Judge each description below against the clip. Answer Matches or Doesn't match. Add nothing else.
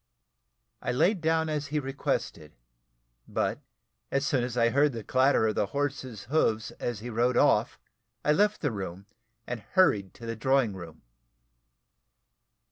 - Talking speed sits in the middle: Matches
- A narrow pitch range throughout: Doesn't match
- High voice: Doesn't match